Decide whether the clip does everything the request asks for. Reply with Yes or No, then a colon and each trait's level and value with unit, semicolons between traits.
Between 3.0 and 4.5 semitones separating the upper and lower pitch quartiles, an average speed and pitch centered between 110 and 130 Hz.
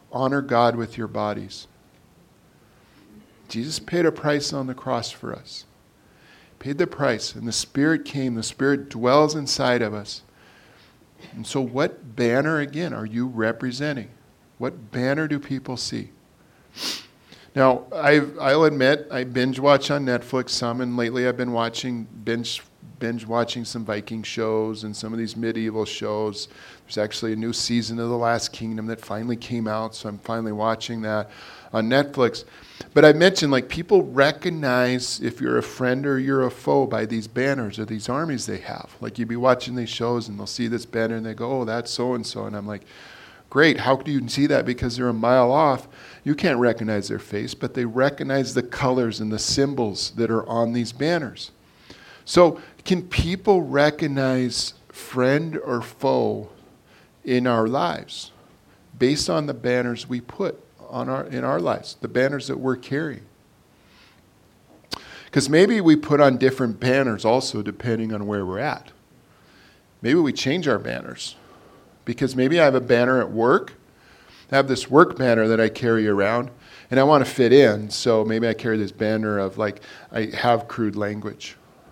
Yes: average, 3.3 semitones; average, 175 wpm; low, 120 Hz